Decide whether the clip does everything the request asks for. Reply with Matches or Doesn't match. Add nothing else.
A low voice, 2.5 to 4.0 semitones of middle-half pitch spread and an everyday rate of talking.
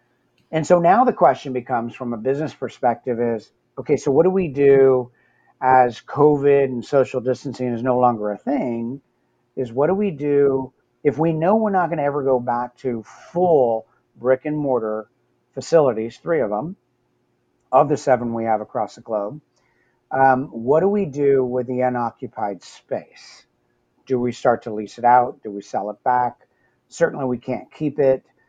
Matches